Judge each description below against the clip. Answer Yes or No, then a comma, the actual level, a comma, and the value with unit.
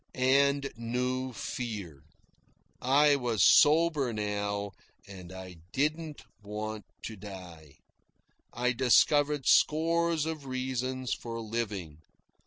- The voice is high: No, low, 125 Hz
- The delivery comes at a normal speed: No, slow, 100 wpm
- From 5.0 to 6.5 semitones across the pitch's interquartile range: Yes, wide, 5.4 semitones